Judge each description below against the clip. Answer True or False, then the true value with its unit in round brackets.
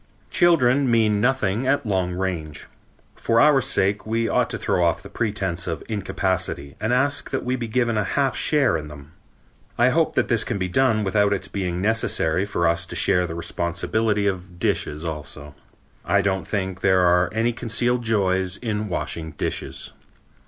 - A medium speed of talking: True (180 wpm)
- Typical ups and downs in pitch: True (4.6 semitones)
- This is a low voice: True (100 Hz)